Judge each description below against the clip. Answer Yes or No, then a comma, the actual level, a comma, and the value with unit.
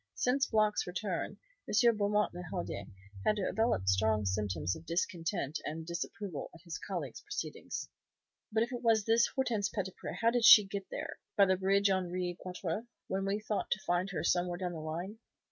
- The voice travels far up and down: No, average, 3.9 semitones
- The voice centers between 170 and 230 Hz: Yes, high, 190 Hz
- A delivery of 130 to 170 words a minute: No, average, 180 wpm